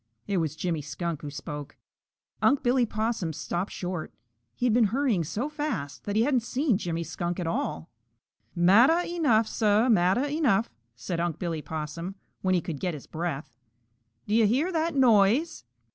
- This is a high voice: Yes, high, 195 Hz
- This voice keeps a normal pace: Yes, average, 170 wpm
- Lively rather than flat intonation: Yes, wide, 6.7 semitones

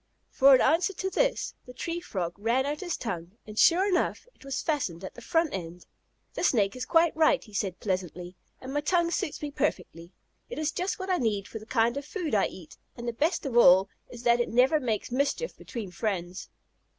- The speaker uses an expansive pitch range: Yes, wide, 8.2 semitones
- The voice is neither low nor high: No, very high, 250 Hz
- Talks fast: Yes, fast, 220 wpm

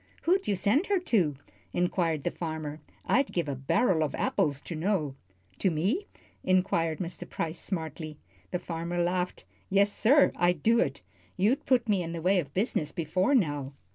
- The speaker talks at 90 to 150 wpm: No, average, 170 wpm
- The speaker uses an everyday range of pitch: Yes, average, 4.3 semitones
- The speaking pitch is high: No, medium, 175 Hz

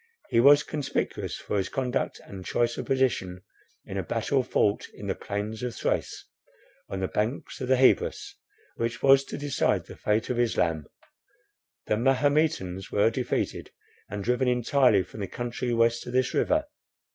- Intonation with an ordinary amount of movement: Yes, average, 4.3 semitones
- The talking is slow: No, average, 165 wpm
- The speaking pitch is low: Yes, low, 120 Hz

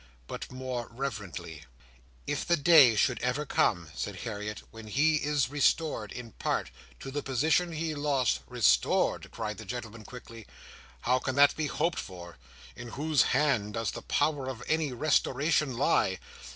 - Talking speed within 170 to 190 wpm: No, average, 155 wpm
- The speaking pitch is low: Yes, low, 130 Hz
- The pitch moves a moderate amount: Yes, average, 5.0 semitones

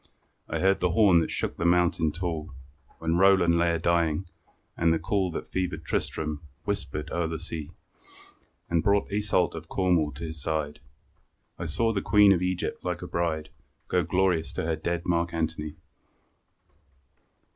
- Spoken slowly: No, average, 165 wpm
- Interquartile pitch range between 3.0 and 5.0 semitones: No, narrow, 2.4 semitones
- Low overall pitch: Yes, very low, 85 Hz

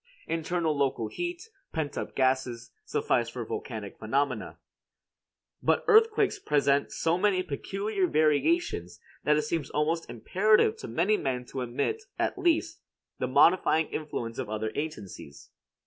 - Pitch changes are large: Yes, wide, 7.2 semitones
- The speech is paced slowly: Yes, slow, 130 wpm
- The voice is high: No, medium, 150 Hz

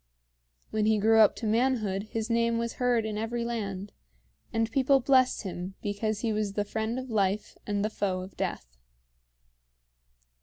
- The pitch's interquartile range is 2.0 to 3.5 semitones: Yes, narrow, 2.4 semitones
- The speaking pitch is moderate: No, high, 220 Hz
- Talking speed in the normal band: Yes, average, 165 wpm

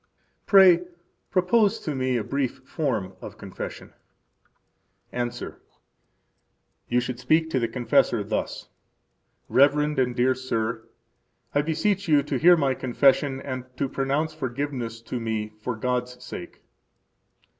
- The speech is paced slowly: Yes, slow, 125 wpm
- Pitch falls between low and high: No, low, 130 Hz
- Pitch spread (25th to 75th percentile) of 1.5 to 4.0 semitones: Yes, average, 3.5 semitones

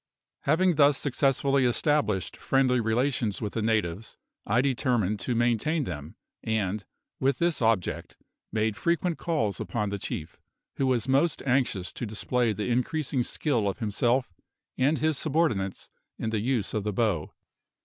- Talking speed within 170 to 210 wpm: No, average, 150 wpm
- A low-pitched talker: Yes, low, 120 Hz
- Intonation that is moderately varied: Yes, average, 4.6 semitones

